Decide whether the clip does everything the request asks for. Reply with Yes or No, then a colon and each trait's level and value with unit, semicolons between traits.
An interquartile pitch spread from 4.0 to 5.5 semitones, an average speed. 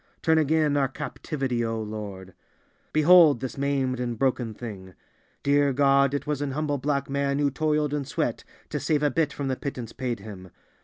No: average, 3.1 semitones; average, 175 wpm